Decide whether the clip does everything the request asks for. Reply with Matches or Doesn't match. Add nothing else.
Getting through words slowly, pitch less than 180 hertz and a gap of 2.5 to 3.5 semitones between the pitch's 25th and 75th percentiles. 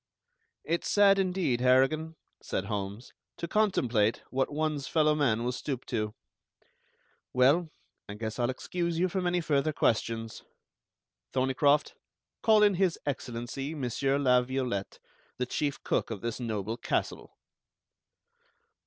Doesn't match